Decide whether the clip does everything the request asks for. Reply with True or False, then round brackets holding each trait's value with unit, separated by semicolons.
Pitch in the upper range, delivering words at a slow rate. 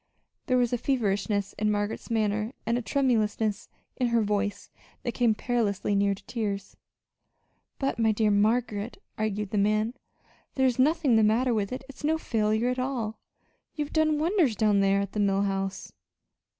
False (220 Hz; 165 wpm)